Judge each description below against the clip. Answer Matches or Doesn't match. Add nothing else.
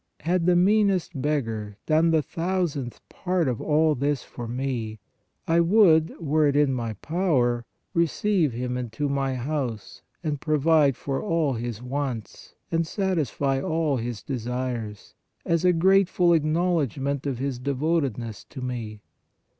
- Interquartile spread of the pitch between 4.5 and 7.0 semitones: Matches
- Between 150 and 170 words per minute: Doesn't match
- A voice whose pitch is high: Doesn't match